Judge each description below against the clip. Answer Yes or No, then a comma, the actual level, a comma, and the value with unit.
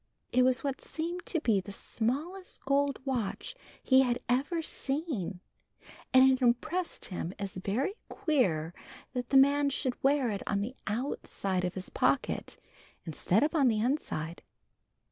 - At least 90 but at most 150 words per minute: Yes, average, 145 wpm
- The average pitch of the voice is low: No, very high, 255 Hz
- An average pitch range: No, wide, 6.0 semitones